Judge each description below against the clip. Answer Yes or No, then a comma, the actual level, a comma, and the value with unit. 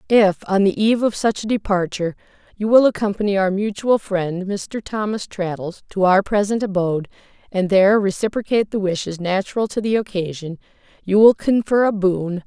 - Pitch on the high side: Yes, high, 200 Hz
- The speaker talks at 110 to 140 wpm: No, average, 170 wpm